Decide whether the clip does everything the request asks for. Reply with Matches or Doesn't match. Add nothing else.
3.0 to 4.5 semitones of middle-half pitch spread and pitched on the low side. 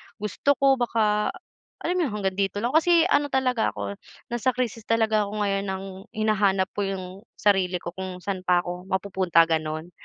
Doesn't match